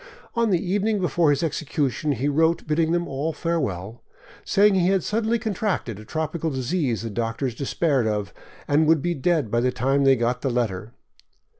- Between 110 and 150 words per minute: No, average, 180 wpm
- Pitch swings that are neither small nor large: No, wide, 5.9 semitones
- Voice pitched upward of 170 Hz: No, medium, 150 Hz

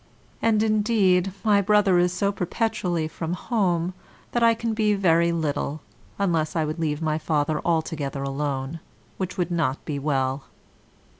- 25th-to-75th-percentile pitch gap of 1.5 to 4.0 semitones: No, average, 4.6 semitones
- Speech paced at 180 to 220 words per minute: No, average, 150 wpm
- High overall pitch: No, medium, 170 Hz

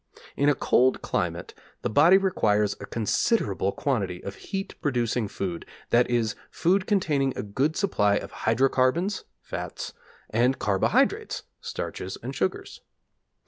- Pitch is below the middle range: Yes, low, 125 Hz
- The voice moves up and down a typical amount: No, wide, 6.3 semitones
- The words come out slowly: Yes, slow, 130 wpm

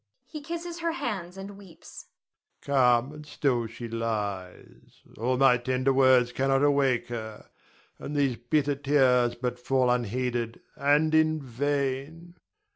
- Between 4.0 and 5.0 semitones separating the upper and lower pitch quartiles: No, average, 3.6 semitones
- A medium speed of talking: No, slow, 130 wpm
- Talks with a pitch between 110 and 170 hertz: Yes, low, 135 Hz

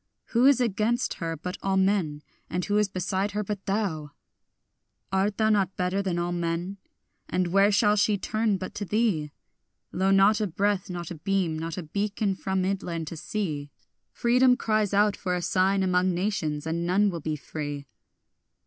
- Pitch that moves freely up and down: No, average, 3.1 semitones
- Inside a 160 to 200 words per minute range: Yes, average, 180 wpm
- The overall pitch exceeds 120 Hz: Yes, high, 190 Hz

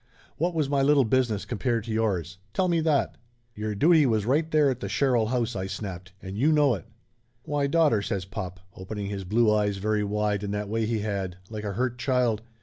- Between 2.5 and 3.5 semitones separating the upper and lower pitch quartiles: No, average, 4.9 semitones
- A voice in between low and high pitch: No, low, 110 Hz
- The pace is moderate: No, fast, 220 wpm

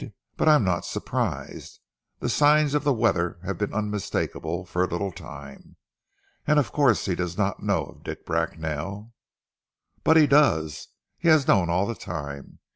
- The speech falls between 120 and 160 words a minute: No, average, 170 wpm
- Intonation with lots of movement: Yes, wide, 8.6 semitones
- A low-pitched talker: Yes, low, 100 Hz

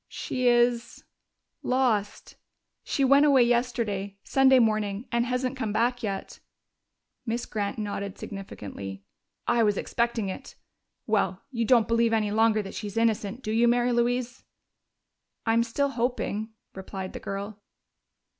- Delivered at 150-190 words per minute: No, slow, 135 wpm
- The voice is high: Yes, high, 230 Hz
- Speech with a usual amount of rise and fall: Yes, average, 3.0 semitones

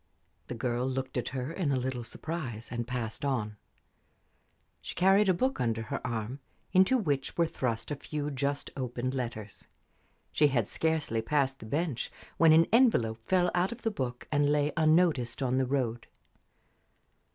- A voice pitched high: No, low, 135 Hz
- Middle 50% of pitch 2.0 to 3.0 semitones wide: No, average, 4.8 semitones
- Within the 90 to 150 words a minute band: No, average, 165 wpm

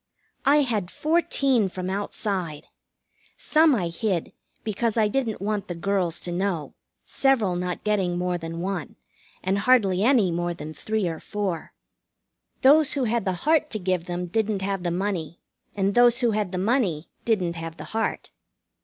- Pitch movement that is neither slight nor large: Yes, average, 4.3 semitones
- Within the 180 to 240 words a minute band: No, average, 165 wpm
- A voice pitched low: No, high, 195 Hz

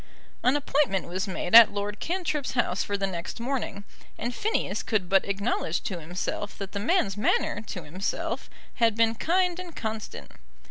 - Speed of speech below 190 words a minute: Yes, average, 170 wpm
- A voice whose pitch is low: No, high, 210 Hz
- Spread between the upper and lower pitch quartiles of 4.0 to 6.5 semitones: Yes, average, 4.9 semitones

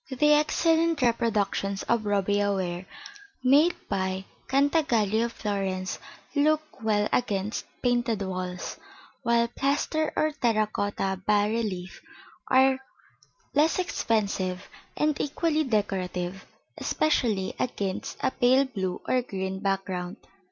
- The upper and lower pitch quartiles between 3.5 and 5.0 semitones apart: No, wide, 5.6 semitones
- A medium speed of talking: No, slow, 110 wpm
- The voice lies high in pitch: Yes, high, 215 Hz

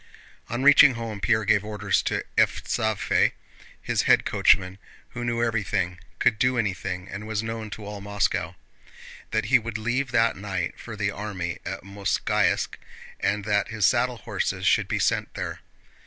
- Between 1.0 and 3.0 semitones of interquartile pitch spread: Yes, narrow, 2.5 semitones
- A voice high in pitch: No, low, 105 Hz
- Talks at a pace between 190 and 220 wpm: No, average, 155 wpm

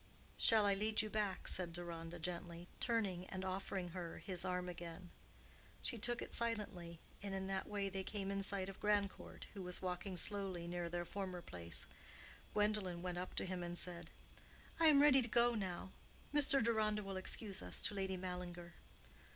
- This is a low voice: No, high, 190 Hz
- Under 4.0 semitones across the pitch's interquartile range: Yes, average, 2.9 semitones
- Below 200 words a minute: Yes, average, 180 wpm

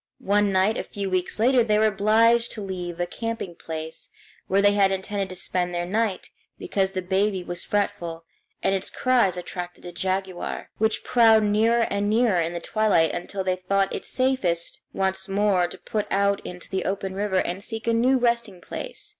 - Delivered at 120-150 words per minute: No, average, 190 wpm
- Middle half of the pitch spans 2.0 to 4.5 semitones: Yes, average, 2.9 semitones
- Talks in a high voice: Yes, high, 195 Hz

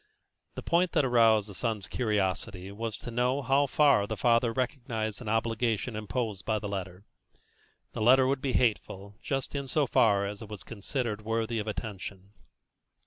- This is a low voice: Yes, low, 115 Hz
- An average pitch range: Yes, average, 3.5 semitones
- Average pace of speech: Yes, average, 170 wpm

